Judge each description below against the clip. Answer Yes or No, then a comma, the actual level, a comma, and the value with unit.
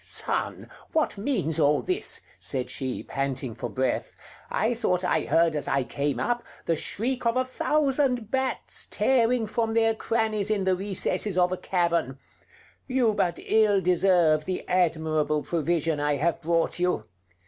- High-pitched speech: No, medium, 180 Hz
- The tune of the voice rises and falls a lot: Yes, wide, 6.4 semitones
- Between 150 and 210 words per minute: Yes, average, 155 wpm